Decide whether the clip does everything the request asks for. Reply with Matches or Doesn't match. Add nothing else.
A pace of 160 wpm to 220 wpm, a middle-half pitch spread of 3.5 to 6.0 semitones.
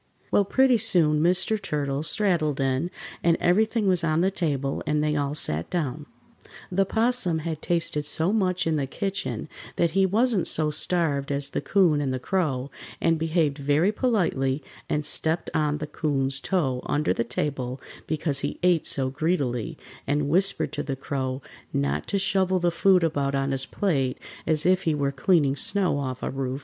Matches